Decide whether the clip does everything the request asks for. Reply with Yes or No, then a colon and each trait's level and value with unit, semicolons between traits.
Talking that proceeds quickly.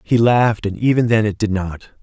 Yes: fast, 235 wpm